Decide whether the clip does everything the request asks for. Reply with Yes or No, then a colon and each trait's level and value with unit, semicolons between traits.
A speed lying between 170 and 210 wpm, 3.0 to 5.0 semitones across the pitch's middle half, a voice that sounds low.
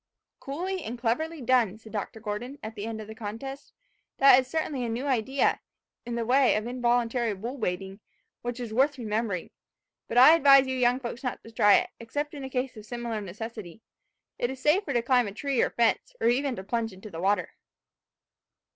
No: average, 200 wpm; average, 3.4 semitones; high, 240 Hz